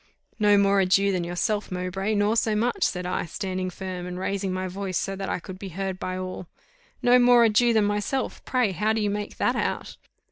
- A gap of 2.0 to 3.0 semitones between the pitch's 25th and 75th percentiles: Yes, narrow, 2.4 semitones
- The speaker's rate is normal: No, fast, 225 wpm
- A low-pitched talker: No, high, 195 Hz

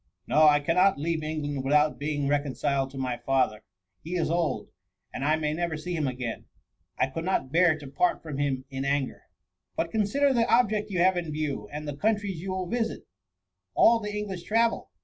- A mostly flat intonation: No, average, 4.9 semitones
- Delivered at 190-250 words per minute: Yes, average, 200 wpm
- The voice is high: No, medium, 155 Hz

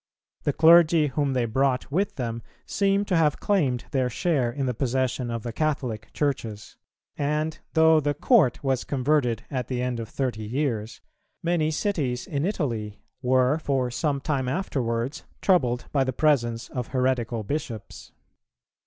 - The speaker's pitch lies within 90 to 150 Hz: Yes, low, 135 Hz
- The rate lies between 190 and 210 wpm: No, average, 155 wpm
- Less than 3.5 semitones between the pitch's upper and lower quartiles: No, average, 4.0 semitones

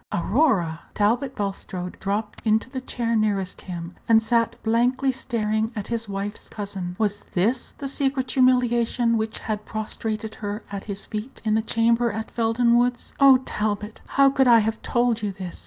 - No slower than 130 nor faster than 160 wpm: No, average, 170 wpm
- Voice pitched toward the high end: Yes, high, 225 Hz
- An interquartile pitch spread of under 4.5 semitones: Yes, average, 2.7 semitones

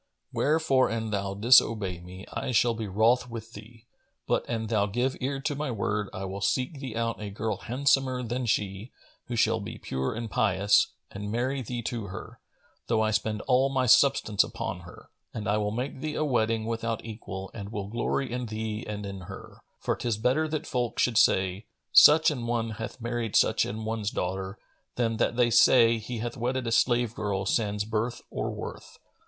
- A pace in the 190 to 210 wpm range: Yes, average, 195 wpm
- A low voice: Yes, low, 115 Hz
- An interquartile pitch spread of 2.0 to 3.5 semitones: Yes, average, 3.0 semitones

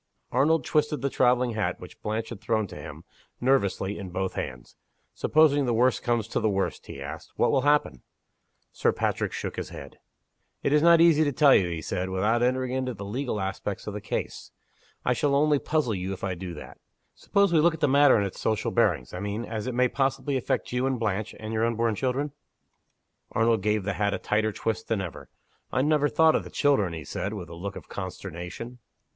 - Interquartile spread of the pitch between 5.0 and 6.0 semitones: Yes, wide, 5.5 semitones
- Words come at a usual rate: No, fast, 215 wpm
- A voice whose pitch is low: Yes, low, 115 Hz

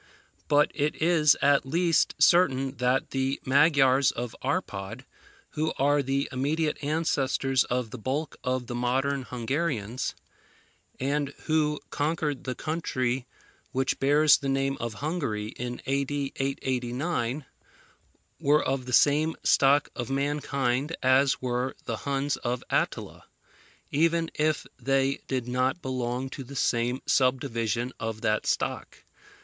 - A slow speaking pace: Yes, slow, 130 wpm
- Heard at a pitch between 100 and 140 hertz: Yes, low, 135 Hz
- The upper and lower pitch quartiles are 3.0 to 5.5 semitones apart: No, narrow, 2.6 semitones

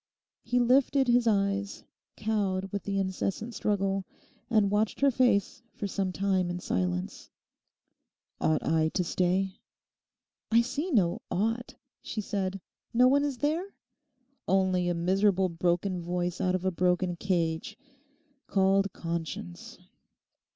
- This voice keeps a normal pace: No, slow, 125 wpm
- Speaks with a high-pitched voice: Yes, high, 195 Hz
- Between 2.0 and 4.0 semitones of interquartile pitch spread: No, average, 4.4 semitones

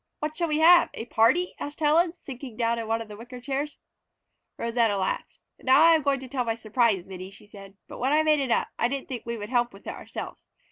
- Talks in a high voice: Yes, high, 245 Hz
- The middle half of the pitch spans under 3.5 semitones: No, average, 4.7 semitones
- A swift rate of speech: Yes, fast, 245 wpm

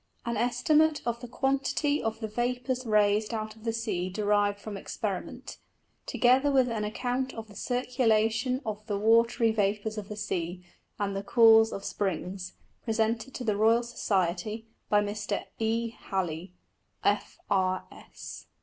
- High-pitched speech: Yes, high, 220 Hz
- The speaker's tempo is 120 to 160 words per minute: Yes, average, 155 wpm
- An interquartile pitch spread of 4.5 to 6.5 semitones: No, average, 2.7 semitones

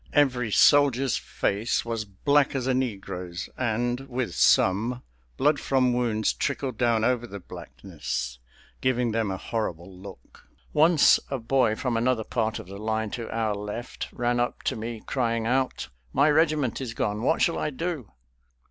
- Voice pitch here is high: No, low, 120 Hz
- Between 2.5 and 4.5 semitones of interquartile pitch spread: Yes, average, 3.4 semitones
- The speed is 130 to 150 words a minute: No, average, 160 wpm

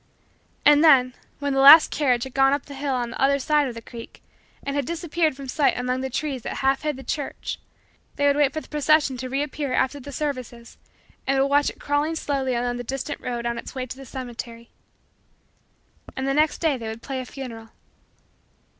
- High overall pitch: Yes, very high, 270 Hz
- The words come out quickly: Yes, fast, 215 wpm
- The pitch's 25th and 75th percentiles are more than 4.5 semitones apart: No, narrow, 2.4 semitones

